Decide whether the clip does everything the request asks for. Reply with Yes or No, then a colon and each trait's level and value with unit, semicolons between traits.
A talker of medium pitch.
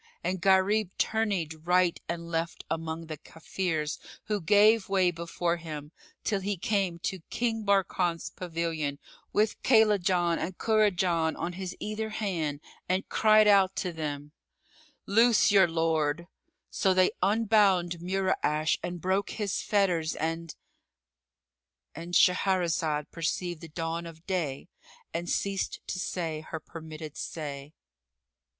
Yes: medium, 175 Hz